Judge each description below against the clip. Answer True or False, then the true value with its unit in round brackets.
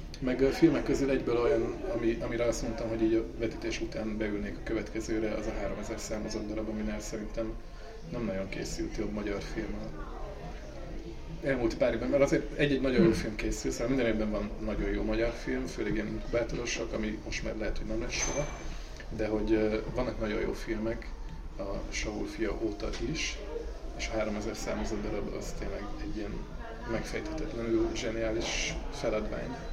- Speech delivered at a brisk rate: True (170 wpm)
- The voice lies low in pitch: True (110 Hz)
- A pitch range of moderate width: False (1.2 semitones)